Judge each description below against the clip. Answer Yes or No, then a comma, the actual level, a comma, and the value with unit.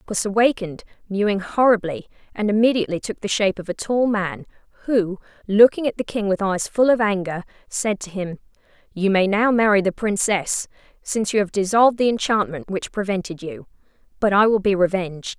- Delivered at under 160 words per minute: No, average, 180 wpm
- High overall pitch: Yes, high, 205 Hz